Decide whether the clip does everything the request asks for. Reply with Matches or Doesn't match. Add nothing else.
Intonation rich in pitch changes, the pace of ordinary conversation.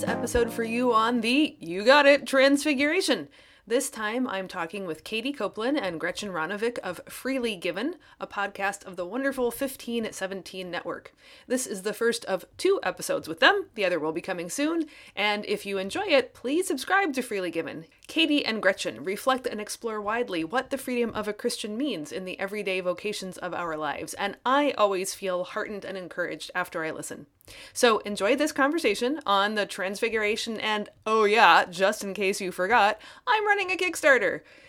Matches